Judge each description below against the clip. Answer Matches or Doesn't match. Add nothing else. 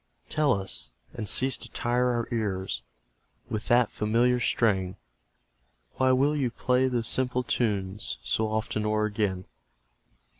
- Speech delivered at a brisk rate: Doesn't match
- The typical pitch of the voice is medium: Doesn't match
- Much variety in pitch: Doesn't match